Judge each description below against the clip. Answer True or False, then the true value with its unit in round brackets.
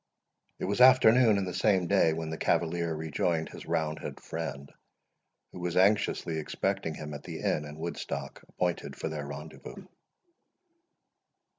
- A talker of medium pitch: False (80 Hz)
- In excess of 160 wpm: False (150 wpm)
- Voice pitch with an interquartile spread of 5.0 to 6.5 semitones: False (3.3 semitones)